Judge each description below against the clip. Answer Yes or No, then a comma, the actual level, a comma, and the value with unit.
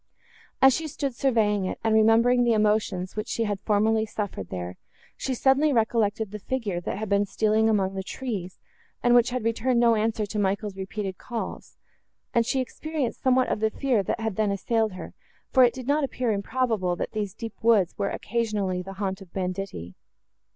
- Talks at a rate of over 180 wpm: Yes, average, 195 wpm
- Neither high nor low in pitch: No, high, 220 Hz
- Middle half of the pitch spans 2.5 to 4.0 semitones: Yes, average, 3.3 semitones